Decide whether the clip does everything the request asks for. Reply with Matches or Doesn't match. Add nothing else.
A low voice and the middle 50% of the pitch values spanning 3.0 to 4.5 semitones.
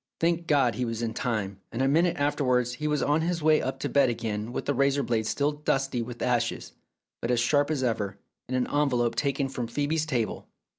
Matches